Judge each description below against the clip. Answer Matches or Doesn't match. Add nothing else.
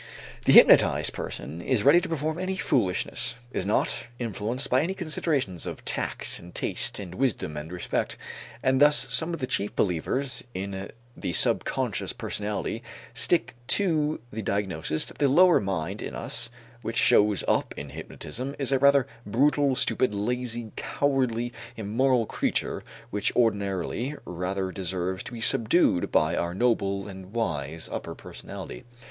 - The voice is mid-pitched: Doesn't match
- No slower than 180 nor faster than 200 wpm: Doesn't match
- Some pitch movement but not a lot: Doesn't match